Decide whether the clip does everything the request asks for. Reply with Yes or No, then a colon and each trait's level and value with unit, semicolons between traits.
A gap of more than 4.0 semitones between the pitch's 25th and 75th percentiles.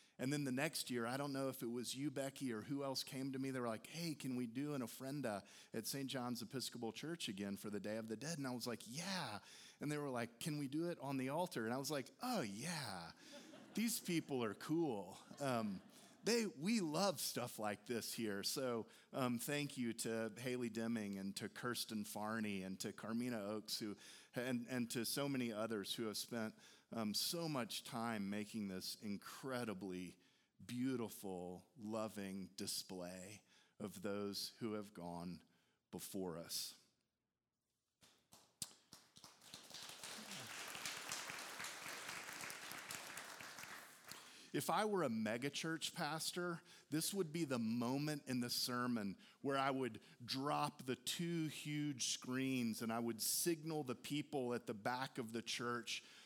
Yes: average, 4.9 semitones